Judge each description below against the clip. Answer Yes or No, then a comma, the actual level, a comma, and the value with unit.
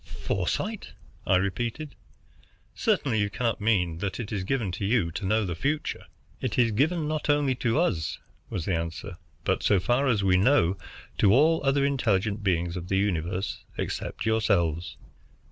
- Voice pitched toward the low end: Yes, low, 105 Hz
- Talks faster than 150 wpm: Yes, average, 160 wpm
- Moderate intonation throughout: No, wide, 6.4 semitones